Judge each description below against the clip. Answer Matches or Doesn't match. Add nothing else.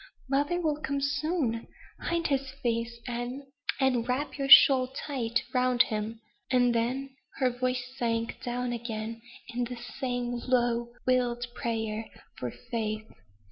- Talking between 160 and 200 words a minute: Doesn't match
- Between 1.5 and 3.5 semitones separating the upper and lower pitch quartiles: Matches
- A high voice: Matches